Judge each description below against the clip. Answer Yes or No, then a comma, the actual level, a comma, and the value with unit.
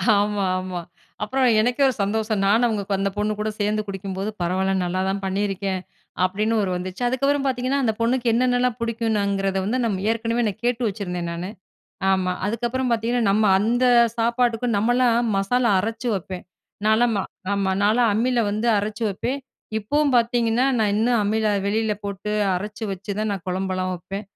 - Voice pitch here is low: No, high, 215 Hz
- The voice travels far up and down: No, average, 3.3 semitones